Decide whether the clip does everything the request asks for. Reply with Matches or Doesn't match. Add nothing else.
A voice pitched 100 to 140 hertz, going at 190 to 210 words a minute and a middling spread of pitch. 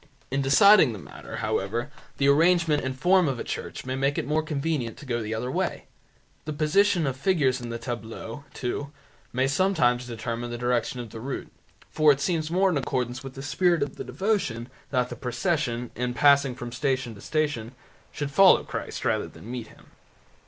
Matches